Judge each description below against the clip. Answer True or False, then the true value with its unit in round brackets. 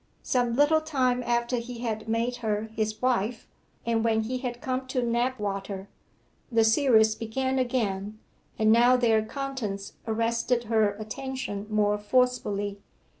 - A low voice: False (230 Hz)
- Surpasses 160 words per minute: False (135 wpm)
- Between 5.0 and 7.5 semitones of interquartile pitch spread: False (2.7 semitones)